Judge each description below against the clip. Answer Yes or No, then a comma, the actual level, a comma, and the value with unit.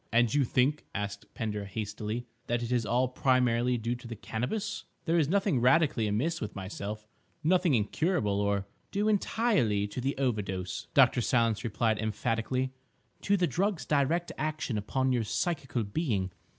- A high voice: No, low, 120 Hz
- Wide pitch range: Yes, wide, 6.1 semitones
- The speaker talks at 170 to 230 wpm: No, average, 150 wpm